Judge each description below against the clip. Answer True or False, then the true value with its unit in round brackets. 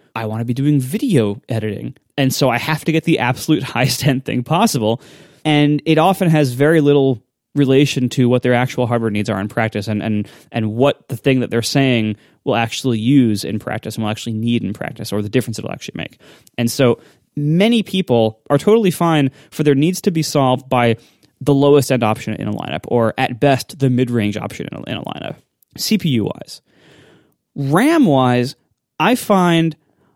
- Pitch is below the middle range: True (130 Hz)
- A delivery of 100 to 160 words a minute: False (200 wpm)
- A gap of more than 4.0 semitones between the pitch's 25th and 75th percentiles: True (4.4 semitones)